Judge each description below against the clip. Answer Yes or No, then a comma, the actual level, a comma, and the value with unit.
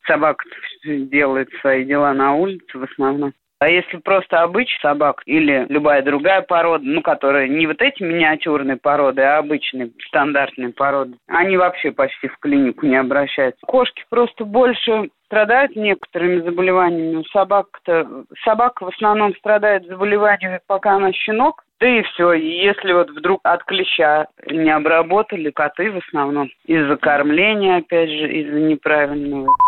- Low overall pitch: No, medium, 170 Hz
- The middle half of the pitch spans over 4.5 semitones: Yes, wide, 5.5 semitones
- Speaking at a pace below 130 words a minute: No, average, 140 wpm